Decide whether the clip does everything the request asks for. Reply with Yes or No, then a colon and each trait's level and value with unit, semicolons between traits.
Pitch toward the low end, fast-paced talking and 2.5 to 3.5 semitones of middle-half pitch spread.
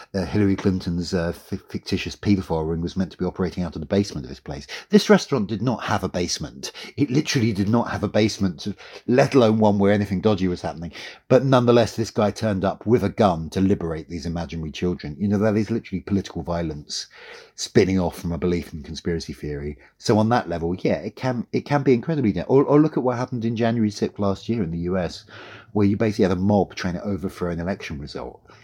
No: low, 100 Hz; fast, 225 wpm; average, 4.3 semitones